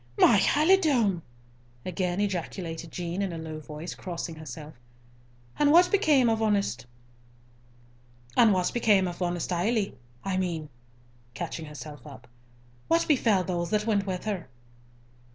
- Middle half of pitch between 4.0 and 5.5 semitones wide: Yes, average, 4.8 semitones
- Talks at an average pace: No, slow, 110 wpm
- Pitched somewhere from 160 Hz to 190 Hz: Yes, medium, 185 Hz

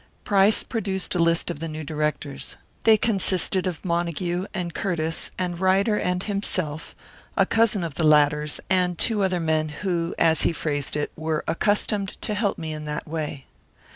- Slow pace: No, average, 170 wpm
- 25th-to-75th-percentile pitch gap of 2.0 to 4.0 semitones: Yes, average, 3.6 semitones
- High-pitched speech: No, medium, 170 Hz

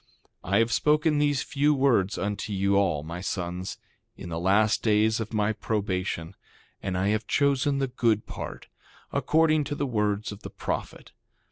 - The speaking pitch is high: No, low, 105 Hz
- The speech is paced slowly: No, average, 170 wpm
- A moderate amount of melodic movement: No, wide, 5.8 semitones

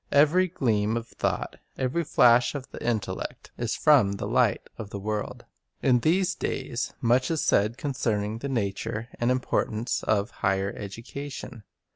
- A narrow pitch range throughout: No, average, 4.2 semitones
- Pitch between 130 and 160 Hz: No, low, 120 Hz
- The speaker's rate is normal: Yes, average, 150 wpm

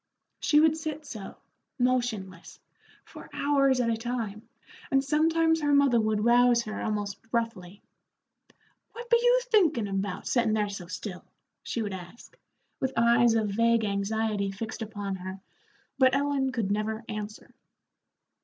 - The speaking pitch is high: Yes, high, 230 Hz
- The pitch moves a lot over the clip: No, average, 4.6 semitones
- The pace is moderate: Yes, average, 145 wpm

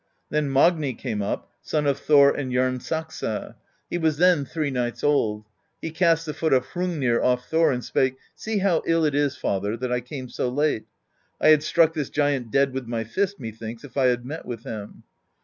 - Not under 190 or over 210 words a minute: Yes, average, 200 wpm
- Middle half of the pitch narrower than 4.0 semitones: No, average, 4.3 semitones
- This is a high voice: No, medium, 140 Hz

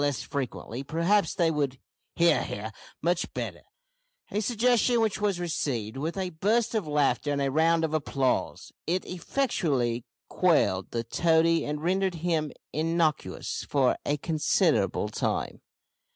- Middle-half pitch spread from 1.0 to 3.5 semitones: No, average, 4.2 semitones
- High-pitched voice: No, medium, 160 Hz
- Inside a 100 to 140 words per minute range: Yes, slow, 135 wpm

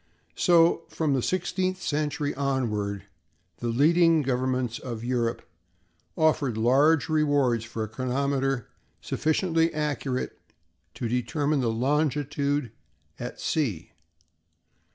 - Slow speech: Yes, slow, 95 wpm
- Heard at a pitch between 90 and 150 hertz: Yes, medium, 140 Hz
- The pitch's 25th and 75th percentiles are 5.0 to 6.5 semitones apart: No, average, 4.0 semitones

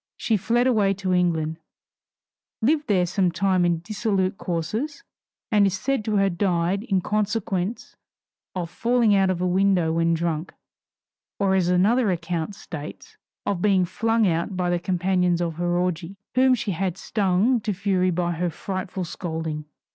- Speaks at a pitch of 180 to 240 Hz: Yes, medium, 185 Hz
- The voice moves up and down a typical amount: Yes, average, 3.0 semitones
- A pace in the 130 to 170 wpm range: Yes, average, 160 wpm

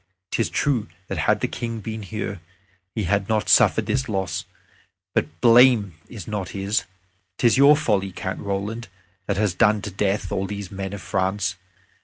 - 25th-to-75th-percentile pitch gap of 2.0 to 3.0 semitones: Yes, narrow, 2.6 semitones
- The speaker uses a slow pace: No, average, 175 wpm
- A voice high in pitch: No, low, 105 Hz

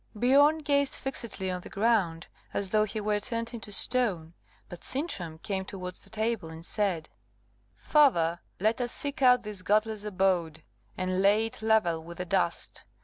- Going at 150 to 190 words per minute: Yes, average, 165 wpm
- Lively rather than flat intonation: No, average, 4.4 semitones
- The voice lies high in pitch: Yes, high, 210 Hz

